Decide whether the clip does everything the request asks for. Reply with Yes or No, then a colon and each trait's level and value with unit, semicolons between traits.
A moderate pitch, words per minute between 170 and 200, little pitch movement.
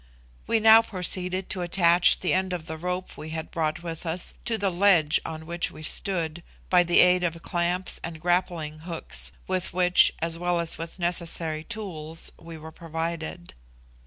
Yes: medium, 175 Hz; average, 175 wpm; narrow, 2.0 semitones